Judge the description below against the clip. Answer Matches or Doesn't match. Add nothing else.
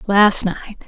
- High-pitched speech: Matches